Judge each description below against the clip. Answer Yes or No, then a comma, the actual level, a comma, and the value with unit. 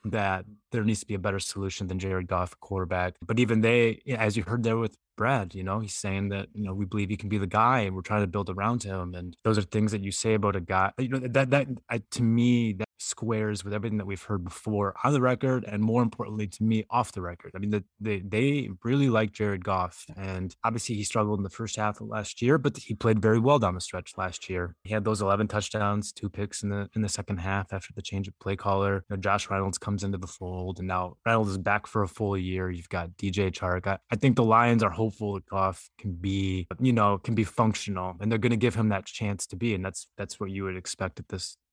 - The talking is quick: Yes, fast, 265 wpm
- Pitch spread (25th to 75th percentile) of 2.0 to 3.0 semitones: Yes, narrow, 2.6 semitones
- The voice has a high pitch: No, low, 105 Hz